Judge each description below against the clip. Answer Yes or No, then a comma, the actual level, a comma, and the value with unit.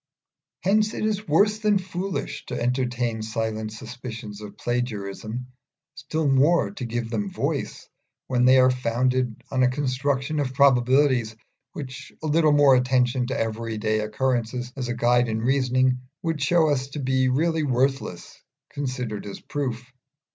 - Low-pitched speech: Yes, low, 130 Hz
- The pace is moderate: Yes, average, 145 wpm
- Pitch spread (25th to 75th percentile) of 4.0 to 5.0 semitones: No, average, 3.1 semitones